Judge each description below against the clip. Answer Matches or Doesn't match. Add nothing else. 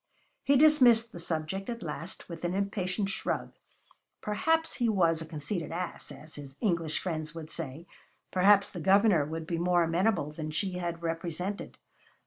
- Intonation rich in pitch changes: Doesn't match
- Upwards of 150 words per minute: Matches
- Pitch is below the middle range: Doesn't match